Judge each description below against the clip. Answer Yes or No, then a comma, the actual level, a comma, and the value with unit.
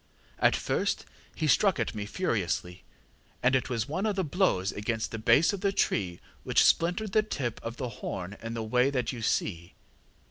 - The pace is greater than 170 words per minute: Yes, average, 190 wpm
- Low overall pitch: Yes, low, 120 Hz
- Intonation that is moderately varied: No, wide, 8.1 semitones